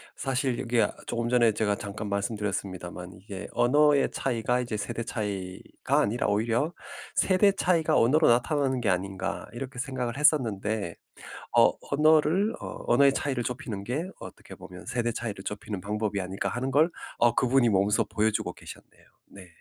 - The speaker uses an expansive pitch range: No, average, 4.8 semitones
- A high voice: No, low, 120 Hz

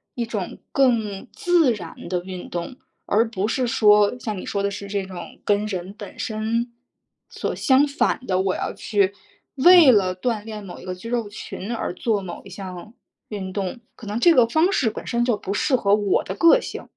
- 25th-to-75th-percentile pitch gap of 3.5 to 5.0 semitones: Yes, average, 3.9 semitones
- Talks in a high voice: Yes, high, 210 Hz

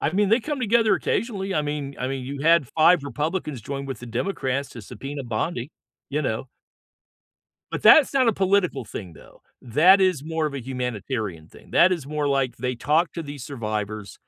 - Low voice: No, medium, 145 Hz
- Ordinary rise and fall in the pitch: No, wide, 5.8 semitones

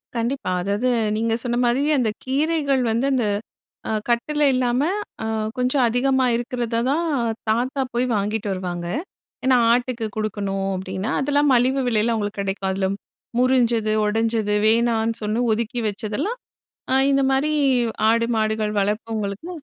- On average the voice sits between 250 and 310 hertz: No, high, 230 Hz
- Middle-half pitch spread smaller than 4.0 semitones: Yes, average, 3.4 semitones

